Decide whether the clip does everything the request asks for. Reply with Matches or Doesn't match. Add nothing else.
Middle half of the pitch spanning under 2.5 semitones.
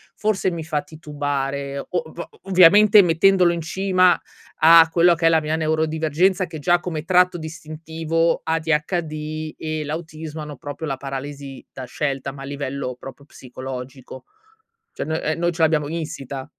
Doesn't match